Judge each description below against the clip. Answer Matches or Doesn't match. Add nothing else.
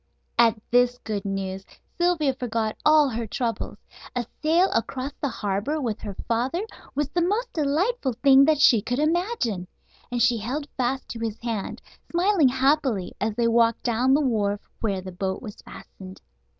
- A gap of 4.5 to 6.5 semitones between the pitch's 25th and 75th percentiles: Matches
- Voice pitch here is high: Matches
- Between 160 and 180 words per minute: Matches